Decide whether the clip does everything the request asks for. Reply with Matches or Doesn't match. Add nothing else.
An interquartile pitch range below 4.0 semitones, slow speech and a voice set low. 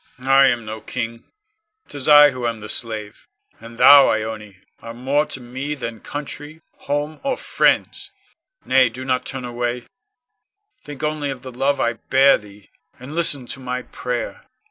Doesn't match